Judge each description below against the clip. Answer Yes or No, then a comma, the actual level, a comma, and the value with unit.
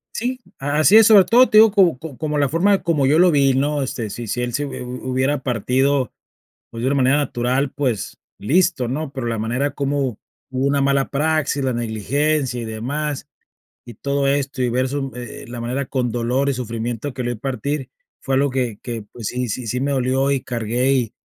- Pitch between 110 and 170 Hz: Yes, low, 135 Hz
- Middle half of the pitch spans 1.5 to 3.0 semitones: Yes, average, 2.7 semitones